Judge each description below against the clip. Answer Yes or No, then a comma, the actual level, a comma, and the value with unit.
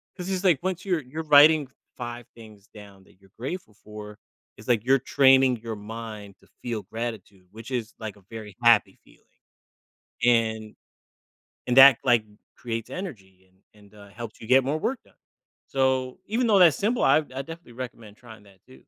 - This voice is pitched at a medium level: No, low, 120 Hz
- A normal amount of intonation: Yes, average, 4.4 semitones